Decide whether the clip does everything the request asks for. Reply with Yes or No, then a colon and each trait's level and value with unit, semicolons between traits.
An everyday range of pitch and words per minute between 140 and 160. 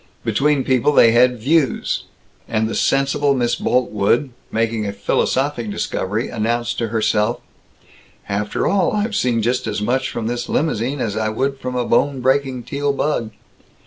Yes: average, 3.7 semitones; average, 155 wpm